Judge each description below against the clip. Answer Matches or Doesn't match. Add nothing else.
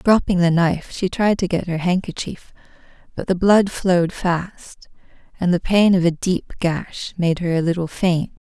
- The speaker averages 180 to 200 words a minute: Matches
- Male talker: Doesn't match